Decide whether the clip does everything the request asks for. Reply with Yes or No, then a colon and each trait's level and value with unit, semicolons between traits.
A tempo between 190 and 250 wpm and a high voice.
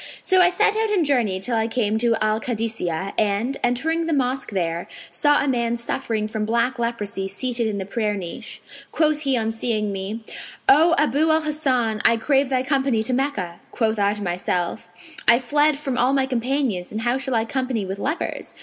Yes: average, 195 wpm; high, 235 Hz